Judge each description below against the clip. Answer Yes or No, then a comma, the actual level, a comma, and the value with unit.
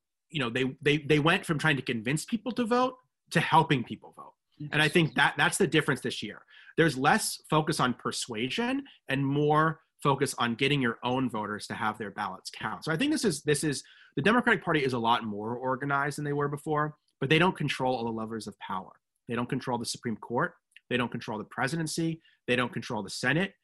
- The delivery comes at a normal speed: No, fast, 225 wpm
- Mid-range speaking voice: Yes, medium, 145 Hz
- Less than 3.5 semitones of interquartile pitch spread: No, average, 4.4 semitones